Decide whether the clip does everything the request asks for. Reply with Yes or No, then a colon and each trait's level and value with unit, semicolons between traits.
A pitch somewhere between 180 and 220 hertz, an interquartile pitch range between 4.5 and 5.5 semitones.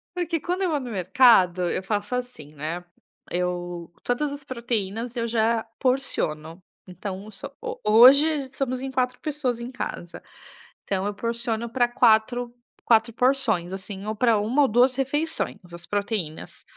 No: high, 230 Hz; average, 5.1 semitones